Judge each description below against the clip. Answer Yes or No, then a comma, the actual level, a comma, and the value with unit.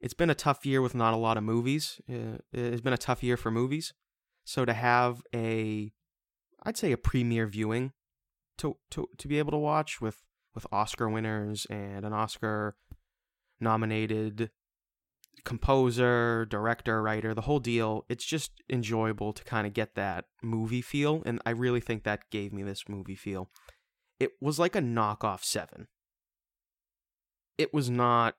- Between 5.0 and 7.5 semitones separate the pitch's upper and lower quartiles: No, average, 2.7 semitones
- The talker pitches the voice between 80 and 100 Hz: No, low, 115 Hz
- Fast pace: No, average, 165 wpm